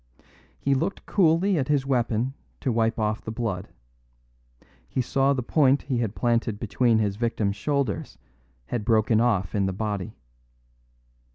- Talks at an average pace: Yes, average, 150 wpm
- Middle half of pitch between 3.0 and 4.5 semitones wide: Yes, average, 3.9 semitones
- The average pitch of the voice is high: No, low, 115 Hz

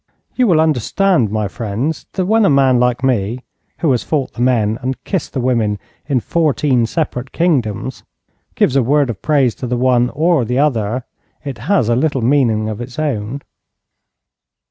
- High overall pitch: No, low, 130 Hz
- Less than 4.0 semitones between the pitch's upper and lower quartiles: No, average, 4.3 semitones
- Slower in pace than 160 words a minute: No, average, 175 wpm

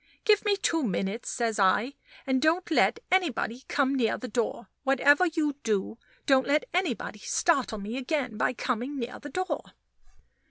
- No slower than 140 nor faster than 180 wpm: Yes, average, 160 wpm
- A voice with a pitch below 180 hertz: No, very high, 265 Hz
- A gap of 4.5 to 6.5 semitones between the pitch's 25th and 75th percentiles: Yes, average, 5.3 semitones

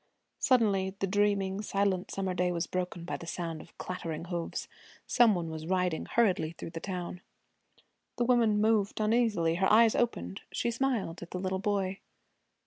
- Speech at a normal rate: Yes, average, 165 wpm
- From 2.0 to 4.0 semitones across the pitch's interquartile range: Yes, average, 3.4 semitones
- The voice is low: No, high, 190 Hz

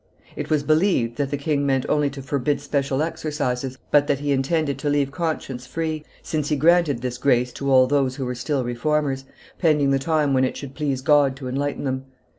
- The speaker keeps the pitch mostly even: Yes, narrow, 2.3 semitones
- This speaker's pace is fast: Yes, fast, 210 wpm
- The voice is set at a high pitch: No, medium, 140 Hz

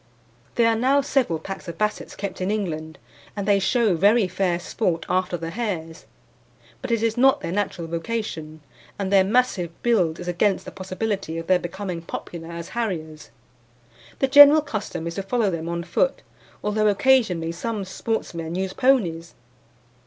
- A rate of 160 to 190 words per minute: Yes, average, 165 wpm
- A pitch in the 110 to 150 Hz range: No, high, 190 Hz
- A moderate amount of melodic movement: Yes, average, 5.0 semitones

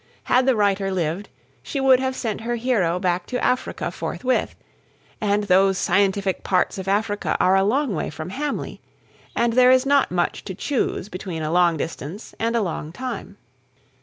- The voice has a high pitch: Yes, high, 205 Hz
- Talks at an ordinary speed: Yes, average, 175 wpm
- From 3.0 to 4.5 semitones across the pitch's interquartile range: No, wide, 5.5 semitones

